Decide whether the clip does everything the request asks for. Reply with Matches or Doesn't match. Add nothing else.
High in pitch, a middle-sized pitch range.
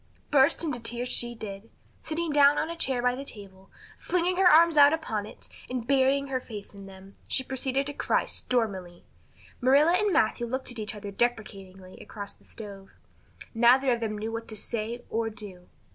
Matches